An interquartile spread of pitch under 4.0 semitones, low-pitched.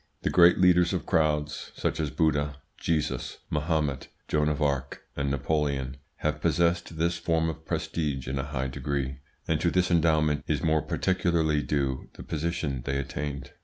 Yes: average, 2.7 semitones; very low, 75 Hz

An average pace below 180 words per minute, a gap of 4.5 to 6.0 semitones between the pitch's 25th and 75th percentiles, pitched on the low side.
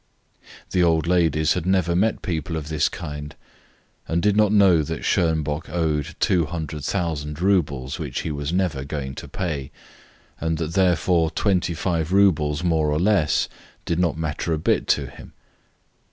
No: average, 155 wpm; average, 3.0 semitones; very low, 80 Hz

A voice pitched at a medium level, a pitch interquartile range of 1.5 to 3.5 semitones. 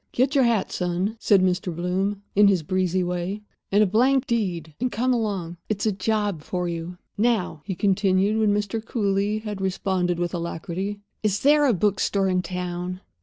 No: high, 195 Hz; average, 3.0 semitones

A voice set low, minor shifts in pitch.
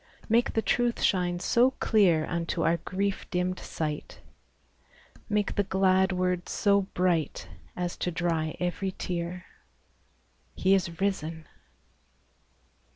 No: medium, 180 Hz; narrow, 2.3 semitones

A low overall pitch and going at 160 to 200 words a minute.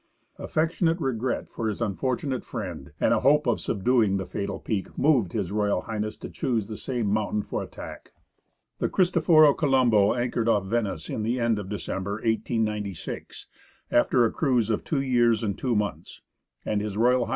Yes: low, 115 Hz; average, 165 wpm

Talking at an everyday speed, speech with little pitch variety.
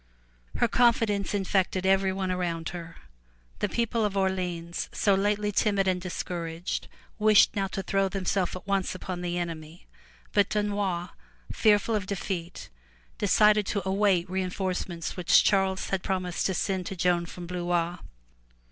Yes: average, 145 wpm; narrow, 2.2 semitones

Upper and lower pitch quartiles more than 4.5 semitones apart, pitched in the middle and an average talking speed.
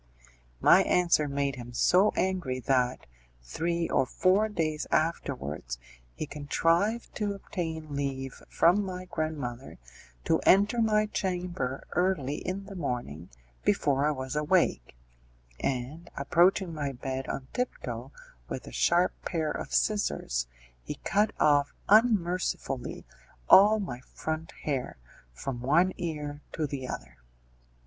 No: wide, 5.6 semitones; medium, 155 Hz; slow, 125 wpm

